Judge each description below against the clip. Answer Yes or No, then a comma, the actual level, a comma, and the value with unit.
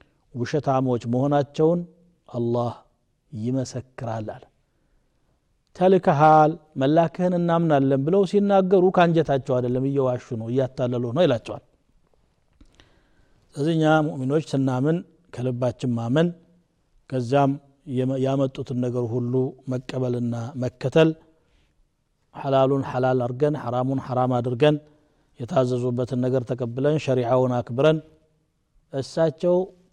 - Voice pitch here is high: No, low, 135 Hz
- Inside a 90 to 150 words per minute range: No, average, 80 wpm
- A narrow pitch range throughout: No, average, 3.9 semitones